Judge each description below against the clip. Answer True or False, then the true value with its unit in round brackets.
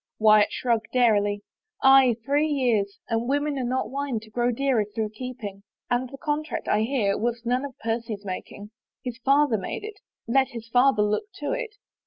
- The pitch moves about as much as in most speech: True (4.0 semitones)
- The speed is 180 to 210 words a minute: True (190 wpm)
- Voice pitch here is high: True (240 Hz)